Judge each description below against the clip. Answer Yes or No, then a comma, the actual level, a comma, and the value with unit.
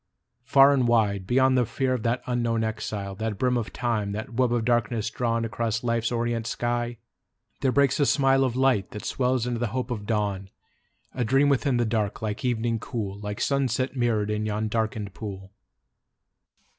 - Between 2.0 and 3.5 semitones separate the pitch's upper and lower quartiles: Yes, average, 2.7 semitones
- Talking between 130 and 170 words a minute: No, average, 180 wpm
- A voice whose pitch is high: No, low, 115 Hz